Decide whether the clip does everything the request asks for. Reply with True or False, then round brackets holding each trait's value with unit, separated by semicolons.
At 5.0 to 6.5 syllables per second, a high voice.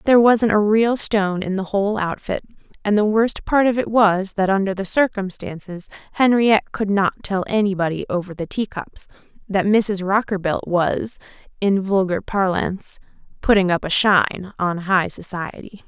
False (4.8 syllables/s; 200 Hz)